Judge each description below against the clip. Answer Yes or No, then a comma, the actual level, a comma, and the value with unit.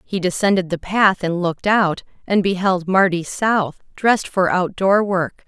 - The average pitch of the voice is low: No, medium, 185 Hz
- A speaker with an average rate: Yes, average, 175 wpm